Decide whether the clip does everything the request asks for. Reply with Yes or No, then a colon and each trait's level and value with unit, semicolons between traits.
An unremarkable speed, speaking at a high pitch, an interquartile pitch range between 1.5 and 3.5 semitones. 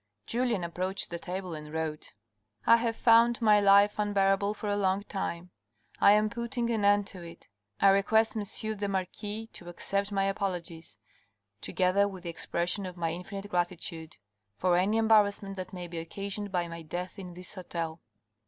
Yes: average, 175 wpm; high, 195 Hz; average, 2.8 semitones